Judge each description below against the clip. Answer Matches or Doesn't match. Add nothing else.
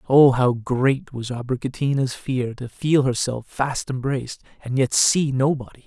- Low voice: Matches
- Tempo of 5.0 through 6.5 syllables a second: Doesn't match